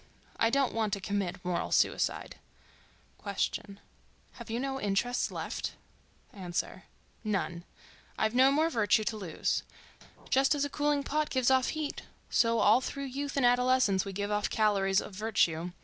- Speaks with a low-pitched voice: No, high, 225 Hz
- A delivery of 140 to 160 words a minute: Yes, average, 150 wpm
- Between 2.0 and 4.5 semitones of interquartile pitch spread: No, average, 5.0 semitones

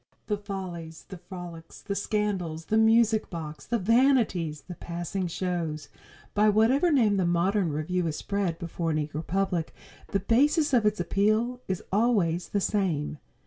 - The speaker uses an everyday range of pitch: Yes, average, 4.3 semitones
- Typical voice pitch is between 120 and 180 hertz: No, high, 190 Hz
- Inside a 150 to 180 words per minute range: Yes, average, 155 wpm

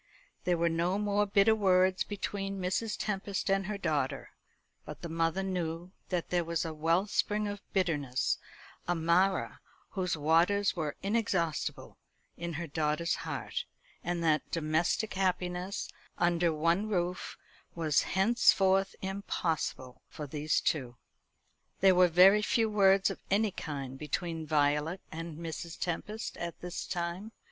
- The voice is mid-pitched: Yes, medium, 175 Hz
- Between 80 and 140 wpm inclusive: Yes, slow, 135 wpm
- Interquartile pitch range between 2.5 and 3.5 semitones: Yes, average, 3.1 semitones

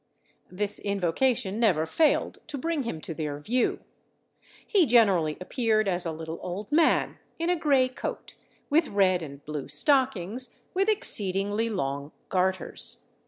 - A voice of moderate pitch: No, high, 205 Hz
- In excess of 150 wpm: No, average, 140 wpm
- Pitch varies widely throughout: Yes, wide, 7.1 semitones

